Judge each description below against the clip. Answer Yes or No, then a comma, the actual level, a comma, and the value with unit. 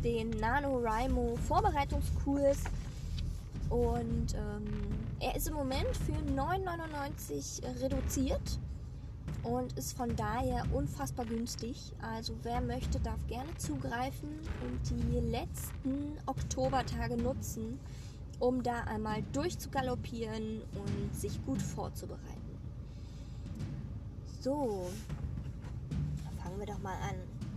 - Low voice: Yes, low, 110 Hz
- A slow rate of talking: Yes, slow, 95 wpm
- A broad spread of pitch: Yes, wide, 7.2 semitones